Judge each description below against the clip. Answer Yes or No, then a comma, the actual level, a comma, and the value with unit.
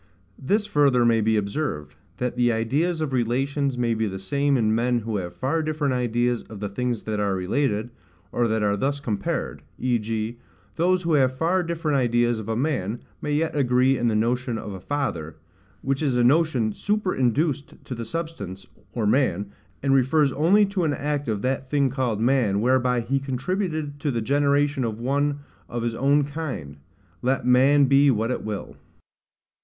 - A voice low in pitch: Yes, low, 130 Hz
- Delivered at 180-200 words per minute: Yes, average, 185 wpm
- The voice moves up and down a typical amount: Yes, average, 4.3 semitones